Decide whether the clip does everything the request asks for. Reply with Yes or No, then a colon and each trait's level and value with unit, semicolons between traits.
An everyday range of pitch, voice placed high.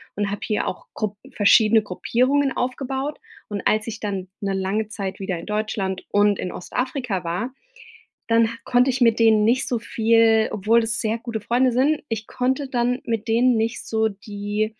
Yes: average, 3.0 semitones; high, 225 Hz